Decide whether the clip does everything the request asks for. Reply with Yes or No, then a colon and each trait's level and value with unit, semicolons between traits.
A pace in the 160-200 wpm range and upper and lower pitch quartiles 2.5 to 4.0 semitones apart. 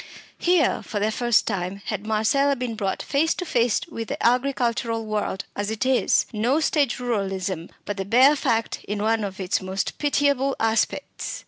No: average, 175 wpm; average, 4.4 semitones